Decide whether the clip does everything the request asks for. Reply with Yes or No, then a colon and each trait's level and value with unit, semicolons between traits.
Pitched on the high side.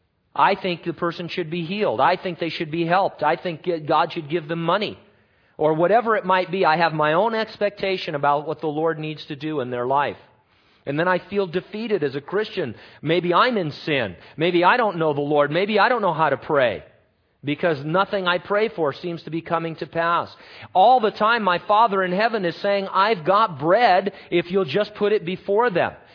No: medium, 175 Hz